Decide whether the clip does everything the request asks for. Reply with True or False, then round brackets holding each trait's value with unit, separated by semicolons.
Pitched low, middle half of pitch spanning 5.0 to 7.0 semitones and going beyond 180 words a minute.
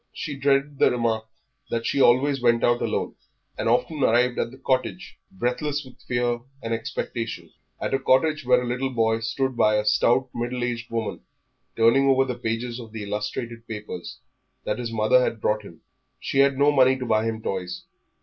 False (120 Hz; 2.7 semitones; 190 wpm)